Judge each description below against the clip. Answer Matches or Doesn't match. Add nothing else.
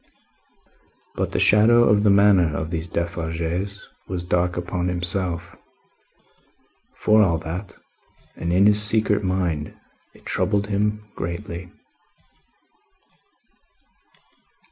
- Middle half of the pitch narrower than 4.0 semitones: Matches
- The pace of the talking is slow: Matches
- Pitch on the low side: Matches